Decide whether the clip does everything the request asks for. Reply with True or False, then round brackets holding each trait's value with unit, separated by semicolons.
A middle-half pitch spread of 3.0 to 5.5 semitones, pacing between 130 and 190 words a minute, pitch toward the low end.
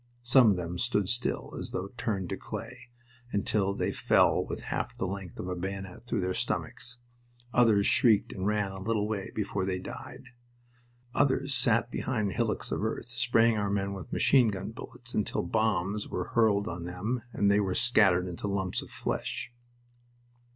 True (3.3 semitones; 175 wpm; 105 Hz)